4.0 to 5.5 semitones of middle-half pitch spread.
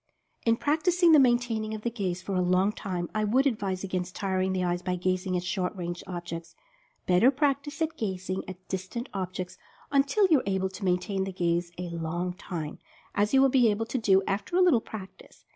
Yes: average, 4.5 semitones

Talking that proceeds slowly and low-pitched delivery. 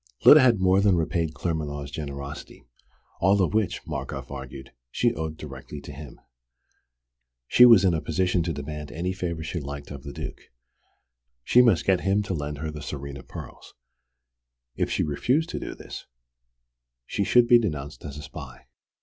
No: average, 170 wpm; very low, 80 Hz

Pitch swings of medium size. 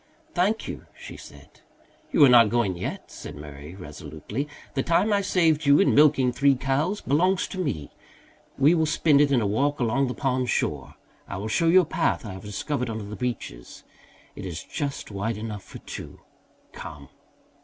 No: wide, 6.7 semitones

